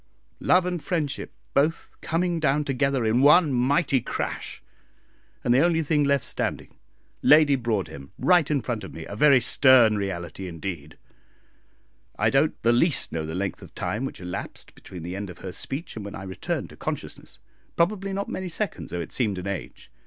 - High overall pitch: No, low, 130 Hz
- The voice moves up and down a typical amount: No, wide, 7.9 semitones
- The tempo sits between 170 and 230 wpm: Yes, average, 180 wpm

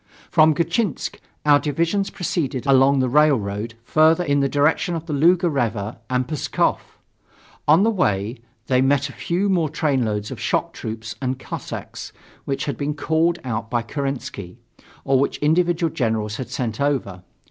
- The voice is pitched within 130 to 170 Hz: Yes, medium, 140 Hz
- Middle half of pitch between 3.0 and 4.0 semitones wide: No, average, 4.9 semitones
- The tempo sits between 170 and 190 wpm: No, average, 160 wpm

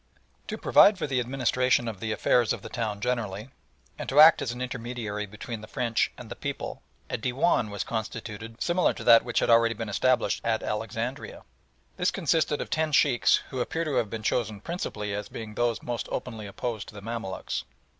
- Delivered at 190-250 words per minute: Yes, average, 195 wpm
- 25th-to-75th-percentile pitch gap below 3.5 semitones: Yes, average, 2.8 semitones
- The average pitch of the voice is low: Yes, low, 115 Hz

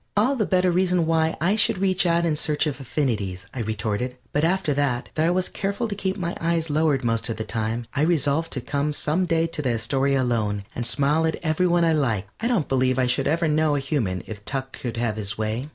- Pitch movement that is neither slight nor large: No, wide, 5.7 semitones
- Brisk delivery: Yes, fast, 240 wpm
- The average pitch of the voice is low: No, medium, 145 Hz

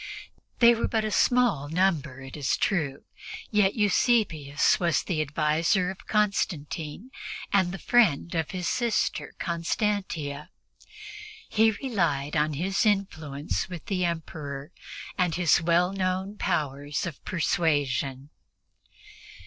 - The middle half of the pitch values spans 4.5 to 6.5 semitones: Yes, average, 4.9 semitones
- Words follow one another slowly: Yes, slow, 115 wpm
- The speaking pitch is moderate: Yes, medium, 170 Hz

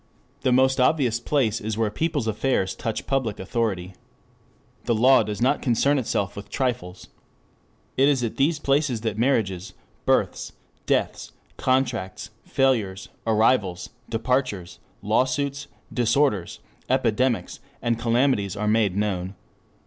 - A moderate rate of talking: No, slow, 110 wpm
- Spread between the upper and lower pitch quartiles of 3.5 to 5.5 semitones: Yes, average, 4.2 semitones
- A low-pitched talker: Yes, low, 115 Hz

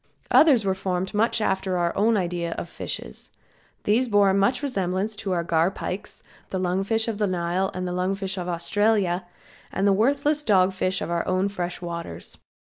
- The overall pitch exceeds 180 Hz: Yes, high, 190 Hz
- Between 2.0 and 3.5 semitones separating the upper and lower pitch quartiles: Yes, narrow, 2.6 semitones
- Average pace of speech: Yes, average, 185 wpm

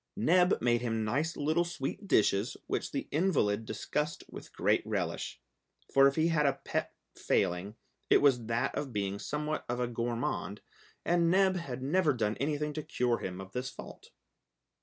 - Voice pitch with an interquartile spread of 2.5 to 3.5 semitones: No, wide, 5.5 semitones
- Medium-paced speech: Yes, average, 170 wpm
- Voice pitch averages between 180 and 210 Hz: No, low, 135 Hz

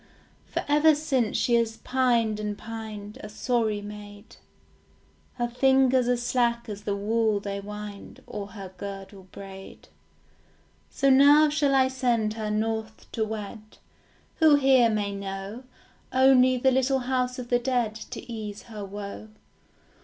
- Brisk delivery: No, average, 145 wpm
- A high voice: Yes, high, 225 Hz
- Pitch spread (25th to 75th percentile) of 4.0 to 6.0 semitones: No, average, 3.6 semitones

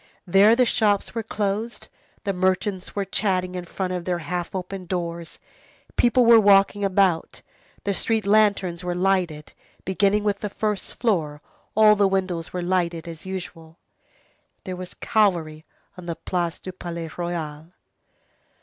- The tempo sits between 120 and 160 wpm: Yes, average, 150 wpm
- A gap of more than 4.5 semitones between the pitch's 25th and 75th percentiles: No, average, 2.8 semitones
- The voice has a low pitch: No, medium, 185 Hz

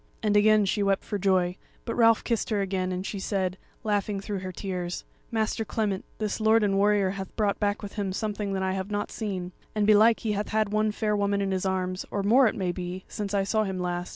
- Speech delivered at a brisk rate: Yes, fast, 235 wpm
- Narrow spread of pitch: Yes, narrow, 2.0 semitones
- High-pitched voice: Yes, high, 200 Hz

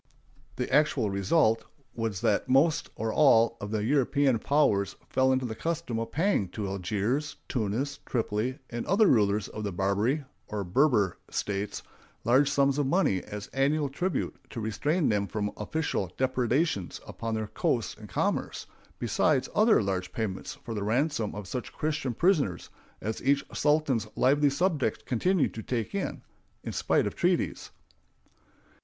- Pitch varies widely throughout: Yes, wide, 5.7 semitones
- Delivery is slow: No, average, 150 wpm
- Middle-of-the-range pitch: No, low, 120 Hz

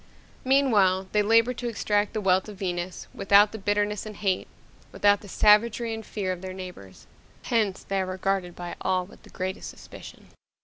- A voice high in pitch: Yes, high, 200 Hz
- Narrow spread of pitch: Yes, narrow, 2.3 semitones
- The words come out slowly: No, average, 180 wpm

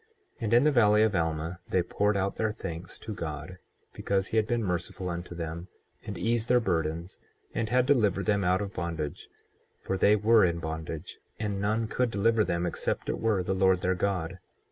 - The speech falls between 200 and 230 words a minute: Yes, fast, 205 wpm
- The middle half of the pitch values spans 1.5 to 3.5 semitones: No, average, 4.1 semitones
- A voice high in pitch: No, very low, 95 Hz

